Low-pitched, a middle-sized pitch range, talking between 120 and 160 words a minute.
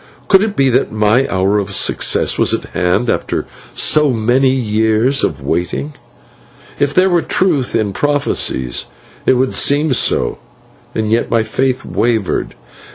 Yes: low, 120 Hz; average, 4.9 semitones; average, 150 wpm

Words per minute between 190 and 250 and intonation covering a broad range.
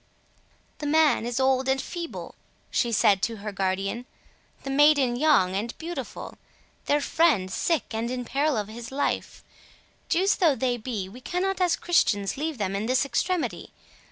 No: average, 155 wpm; wide, 6.0 semitones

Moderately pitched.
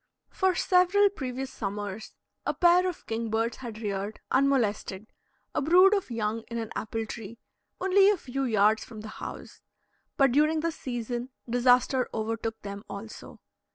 No: high, 240 Hz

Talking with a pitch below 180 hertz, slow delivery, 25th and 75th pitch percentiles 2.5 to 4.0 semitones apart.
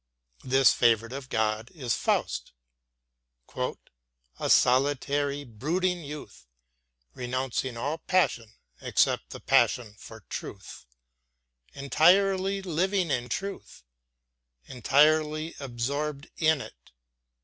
No: medium, 140 Hz; slow, 90 wpm; average, 4.9 semitones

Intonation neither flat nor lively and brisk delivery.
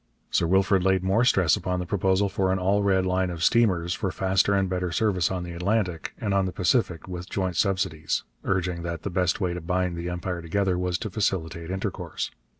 No: narrow, 1.7 semitones; fast, 210 wpm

